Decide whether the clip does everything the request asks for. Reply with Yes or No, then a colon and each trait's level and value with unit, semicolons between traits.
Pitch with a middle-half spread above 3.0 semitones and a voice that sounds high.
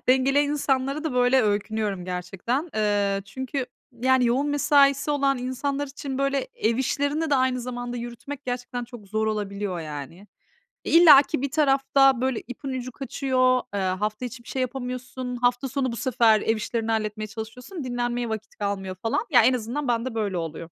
Yes: average, 3.8 semitones; very high, 250 Hz